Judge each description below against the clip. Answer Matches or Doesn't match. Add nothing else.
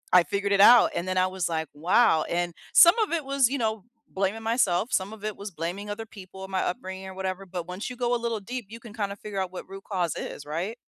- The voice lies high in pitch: Matches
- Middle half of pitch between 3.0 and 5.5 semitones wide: Matches